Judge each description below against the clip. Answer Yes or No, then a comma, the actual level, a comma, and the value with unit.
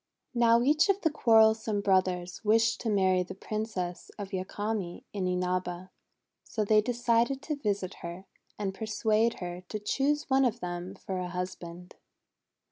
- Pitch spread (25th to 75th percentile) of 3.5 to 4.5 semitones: Yes, average, 4.0 semitones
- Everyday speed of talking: Yes, average, 150 wpm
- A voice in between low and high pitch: No, high, 210 Hz